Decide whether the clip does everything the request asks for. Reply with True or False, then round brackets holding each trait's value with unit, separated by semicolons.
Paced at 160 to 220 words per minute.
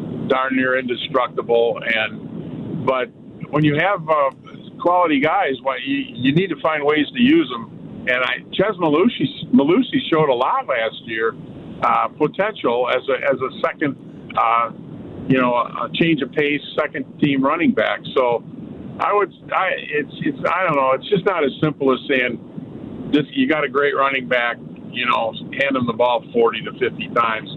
True (175 wpm)